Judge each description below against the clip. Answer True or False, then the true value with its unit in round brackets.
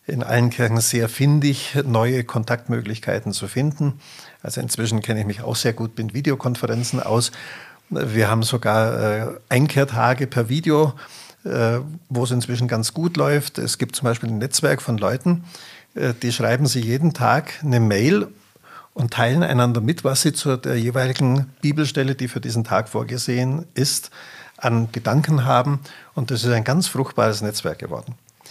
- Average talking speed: True (155 wpm)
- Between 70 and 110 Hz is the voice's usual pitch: False (125 Hz)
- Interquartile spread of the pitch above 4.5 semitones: False (3.2 semitones)